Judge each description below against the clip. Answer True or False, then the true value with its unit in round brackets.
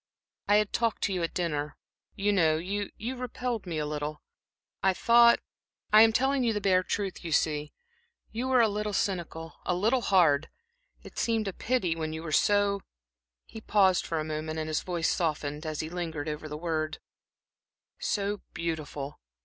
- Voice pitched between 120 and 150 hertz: False (180 Hz)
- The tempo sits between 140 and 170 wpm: False (180 wpm)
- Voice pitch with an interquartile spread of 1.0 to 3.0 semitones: False (5.0 semitones)